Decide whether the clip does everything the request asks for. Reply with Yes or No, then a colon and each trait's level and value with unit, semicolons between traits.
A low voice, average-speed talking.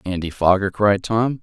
Yes: low, 100 Hz; average, 170 wpm